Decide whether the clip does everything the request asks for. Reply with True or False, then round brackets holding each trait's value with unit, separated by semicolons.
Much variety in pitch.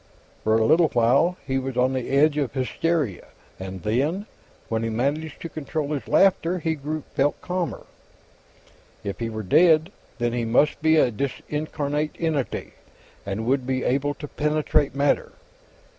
False (4.5 semitones)